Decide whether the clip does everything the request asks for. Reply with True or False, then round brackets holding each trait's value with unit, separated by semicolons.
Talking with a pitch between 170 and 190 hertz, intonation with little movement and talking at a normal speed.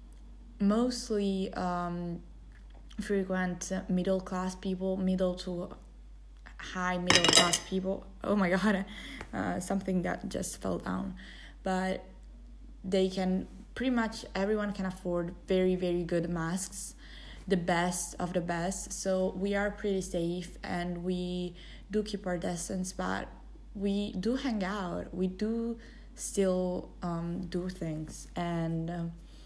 False (185 Hz; 2.0 semitones; 125 wpm)